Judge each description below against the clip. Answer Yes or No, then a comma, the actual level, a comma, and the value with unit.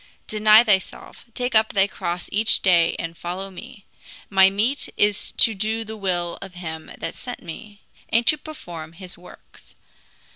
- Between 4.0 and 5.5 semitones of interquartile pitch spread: No, average, 3.6 semitones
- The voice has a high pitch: Yes, high, 195 Hz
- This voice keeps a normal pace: Yes, average, 160 wpm